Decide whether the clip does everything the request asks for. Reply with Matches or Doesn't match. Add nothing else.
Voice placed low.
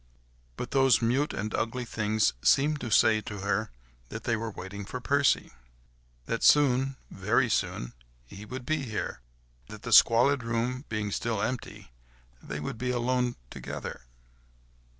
Matches